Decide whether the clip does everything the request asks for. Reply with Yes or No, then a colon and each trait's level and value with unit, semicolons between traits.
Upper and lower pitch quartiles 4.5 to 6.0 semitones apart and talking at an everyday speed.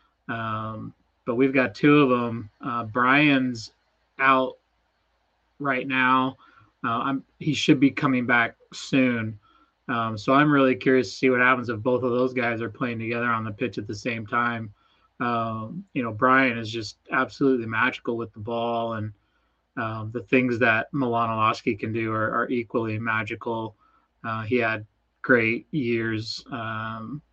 No: narrow, 2.6 semitones; average, 160 wpm